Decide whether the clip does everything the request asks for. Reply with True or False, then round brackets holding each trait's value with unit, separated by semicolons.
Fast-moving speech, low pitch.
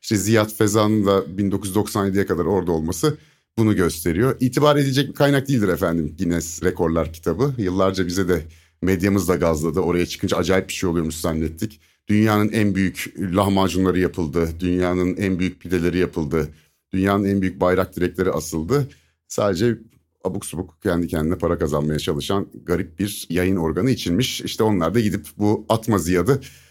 True (155 wpm; 95 Hz)